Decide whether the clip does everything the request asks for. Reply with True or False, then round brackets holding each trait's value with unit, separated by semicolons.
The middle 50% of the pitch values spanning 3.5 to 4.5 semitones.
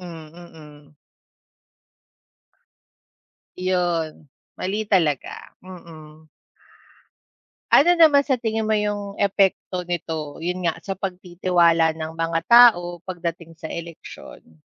False (3.1 semitones)